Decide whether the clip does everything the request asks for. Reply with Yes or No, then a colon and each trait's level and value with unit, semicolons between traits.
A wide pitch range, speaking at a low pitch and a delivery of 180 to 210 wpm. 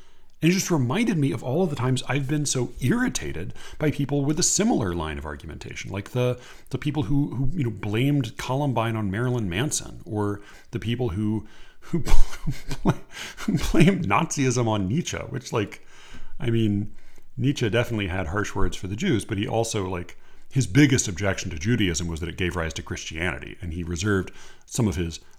Yes: wide, 5.7 semitones; low, 110 Hz; average, 185 wpm